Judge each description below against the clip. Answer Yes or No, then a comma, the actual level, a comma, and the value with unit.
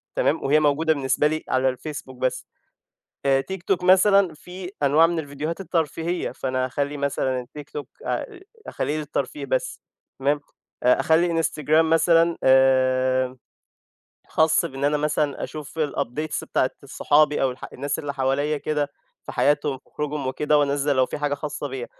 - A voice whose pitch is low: No, medium, 145 Hz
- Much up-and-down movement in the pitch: No, average, 2.9 semitones